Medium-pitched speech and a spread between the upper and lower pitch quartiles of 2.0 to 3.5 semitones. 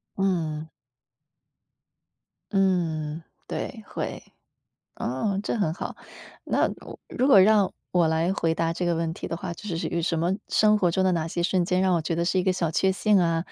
Yes: medium, 175 Hz; narrow, 2.5 semitones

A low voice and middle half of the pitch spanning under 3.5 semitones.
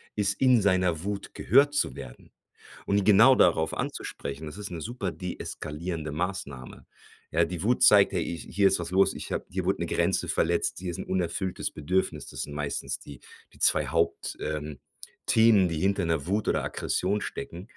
No: very low, 90 Hz; average, 4.1 semitones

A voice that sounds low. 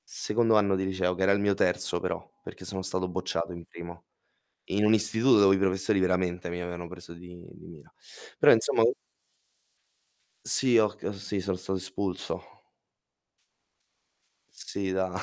Yes: very low, 95 Hz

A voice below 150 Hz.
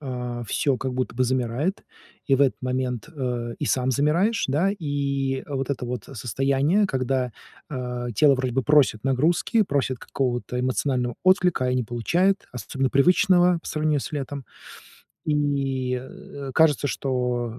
Yes: low, 135 Hz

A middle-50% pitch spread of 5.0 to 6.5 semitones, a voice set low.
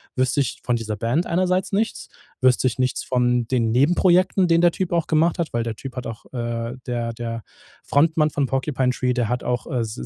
Yes: wide, 5.5 semitones; low, 130 Hz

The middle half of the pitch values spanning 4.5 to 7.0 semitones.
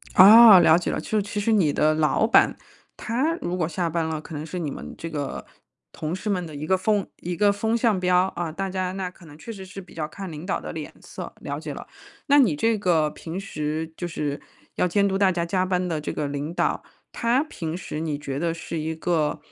No: average, 3.9 semitones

